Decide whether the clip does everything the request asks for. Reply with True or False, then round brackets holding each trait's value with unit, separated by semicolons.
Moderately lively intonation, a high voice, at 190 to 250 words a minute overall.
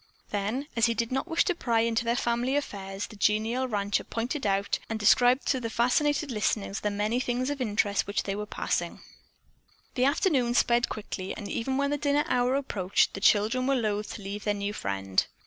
True (3.9 semitones; 230 Hz; 200 wpm)